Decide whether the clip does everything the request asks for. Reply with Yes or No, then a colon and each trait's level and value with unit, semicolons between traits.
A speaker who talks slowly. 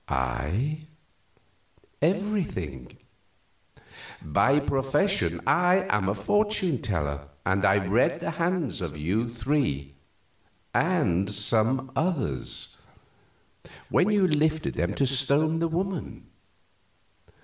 Yes: slow, 95 wpm